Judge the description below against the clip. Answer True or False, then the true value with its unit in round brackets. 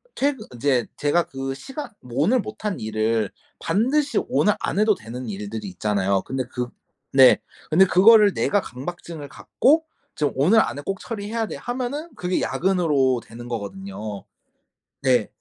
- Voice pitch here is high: False (150 Hz)